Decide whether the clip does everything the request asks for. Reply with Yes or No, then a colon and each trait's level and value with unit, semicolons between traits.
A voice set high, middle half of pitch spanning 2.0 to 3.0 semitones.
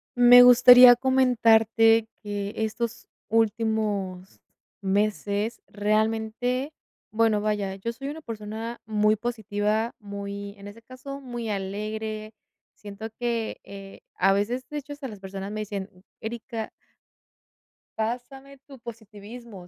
Yes: high, 220 Hz; average, 2.7 semitones